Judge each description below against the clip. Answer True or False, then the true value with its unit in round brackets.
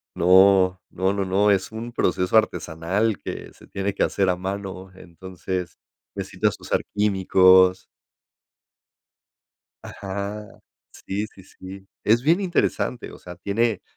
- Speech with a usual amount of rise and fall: False (2.0 semitones)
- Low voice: True (95 Hz)